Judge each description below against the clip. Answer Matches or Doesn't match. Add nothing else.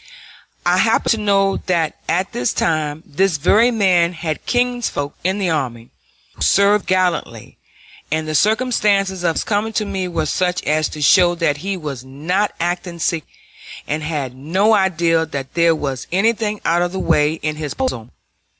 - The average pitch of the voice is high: Doesn't match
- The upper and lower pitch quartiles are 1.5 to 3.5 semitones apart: Doesn't match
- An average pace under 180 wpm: Matches